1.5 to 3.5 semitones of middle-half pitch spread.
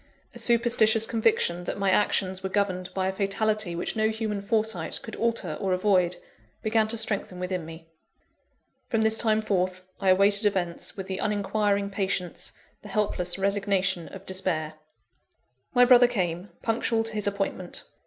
Yes: average, 2.8 semitones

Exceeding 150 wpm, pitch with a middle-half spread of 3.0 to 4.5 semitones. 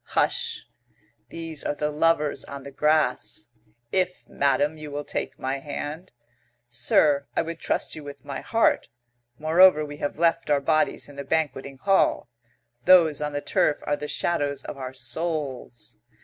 No: average, 165 wpm; narrow, 2.5 semitones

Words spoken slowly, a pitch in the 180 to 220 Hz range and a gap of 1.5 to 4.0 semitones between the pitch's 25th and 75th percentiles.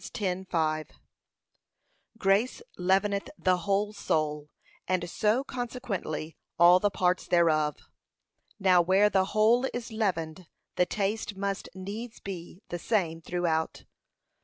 Yes: slow, 110 wpm; high, 190 Hz; average, 3.3 semitones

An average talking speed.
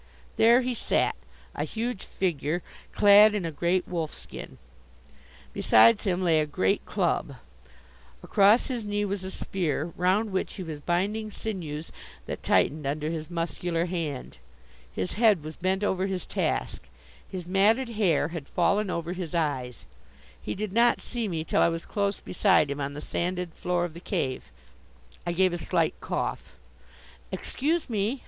Yes: average, 160 wpm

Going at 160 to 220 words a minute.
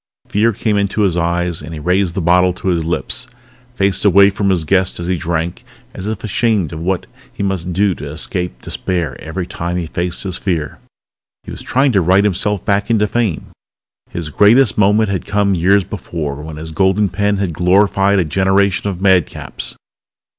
Yes: average, 190 wpm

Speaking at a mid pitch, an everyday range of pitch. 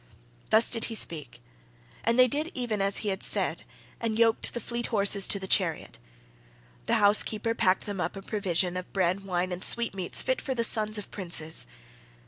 No: high, 205 Hz; average, 3.6 semitones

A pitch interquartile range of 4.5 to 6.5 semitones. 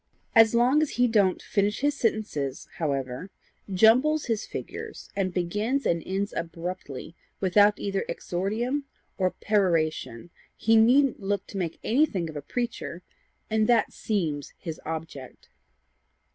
Yes: average, 5.2 semitones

